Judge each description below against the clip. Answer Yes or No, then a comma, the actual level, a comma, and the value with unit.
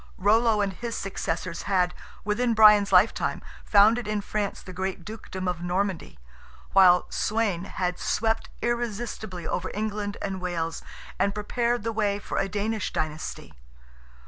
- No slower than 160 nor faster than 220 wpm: No, average, 140 wpm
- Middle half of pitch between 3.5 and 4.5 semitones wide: No, average, 3.0 semitones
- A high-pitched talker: Yes, high, 200 Hz